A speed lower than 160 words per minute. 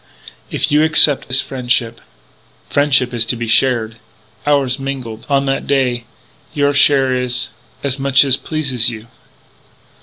Yes: average, 140 wpm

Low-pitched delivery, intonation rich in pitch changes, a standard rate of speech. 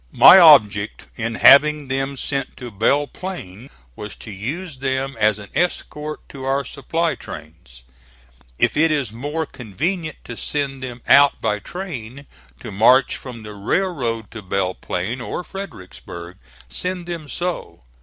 Yes: low, 130 Hz; wide, 6.1 semitones; average, 145 wpm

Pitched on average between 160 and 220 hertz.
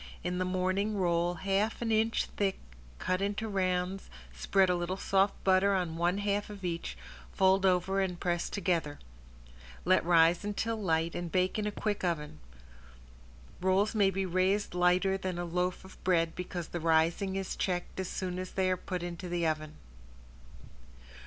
Yes: medium, 185 Hz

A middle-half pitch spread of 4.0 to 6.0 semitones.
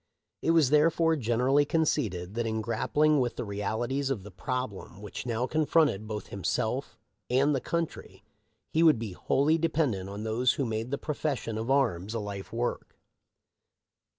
Yes: wide, 5.4 semitones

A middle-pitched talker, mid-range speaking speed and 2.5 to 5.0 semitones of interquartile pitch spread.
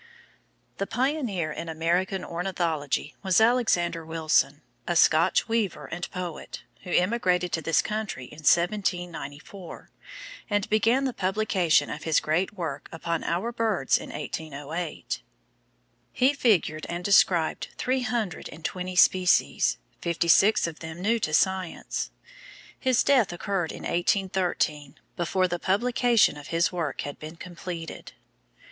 No: medium, 180 Hz; slow, 130 wpm; average, 4.0 semitones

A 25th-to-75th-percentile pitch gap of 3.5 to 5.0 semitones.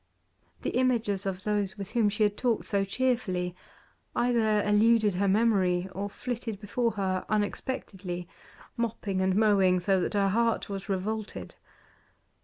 No: average, 2.8 semitones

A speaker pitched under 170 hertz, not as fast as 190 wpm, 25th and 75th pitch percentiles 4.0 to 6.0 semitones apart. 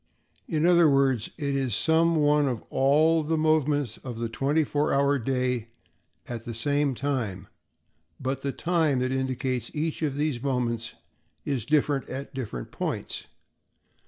No: medium, 140 Hz; average, 150 wpm; average, 3.0 semitones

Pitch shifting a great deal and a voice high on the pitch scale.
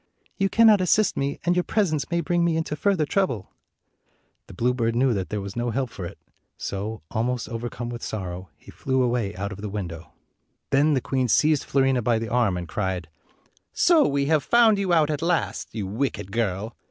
No: wide, 6.9 semitones; low, 125 Hz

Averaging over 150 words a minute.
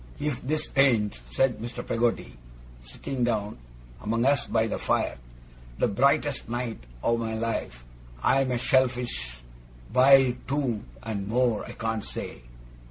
No: slow, 135 wpm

